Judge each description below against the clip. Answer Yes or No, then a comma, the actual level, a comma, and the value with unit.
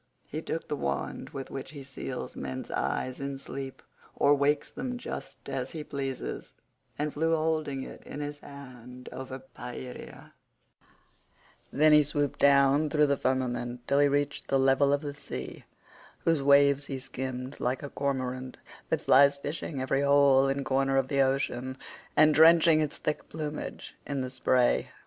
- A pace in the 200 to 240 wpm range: No, average, 165 wpm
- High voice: No, medium, 140 Hz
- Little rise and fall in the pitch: Yes, narrow, 1.9 semitones